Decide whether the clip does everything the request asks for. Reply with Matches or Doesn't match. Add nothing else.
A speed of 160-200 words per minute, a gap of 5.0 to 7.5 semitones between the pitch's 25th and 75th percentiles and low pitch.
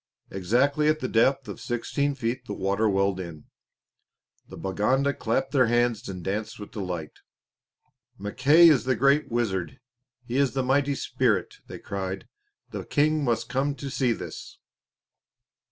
Doesn't match